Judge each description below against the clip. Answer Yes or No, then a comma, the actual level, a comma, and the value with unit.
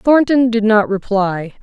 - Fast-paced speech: No, average, 150 wpm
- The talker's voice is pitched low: No, high, 220 Hz